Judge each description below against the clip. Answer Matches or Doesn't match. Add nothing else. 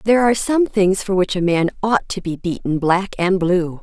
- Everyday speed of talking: Doesn't match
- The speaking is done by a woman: Matches